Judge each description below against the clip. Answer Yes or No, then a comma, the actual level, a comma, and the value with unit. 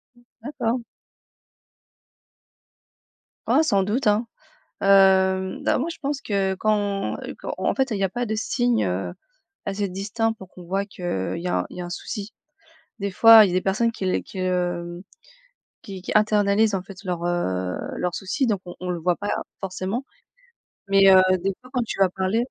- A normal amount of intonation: Yes, average, 3.0 semitones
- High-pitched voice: Yes, high, 195 Hz